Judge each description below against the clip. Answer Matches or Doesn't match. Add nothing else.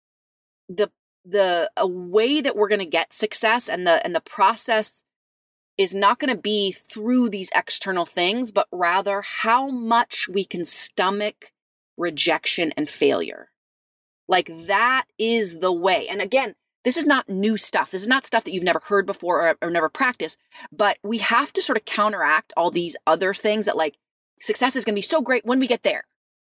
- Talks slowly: Doesn't match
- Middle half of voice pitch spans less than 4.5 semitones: Doesn't match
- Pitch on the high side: Matches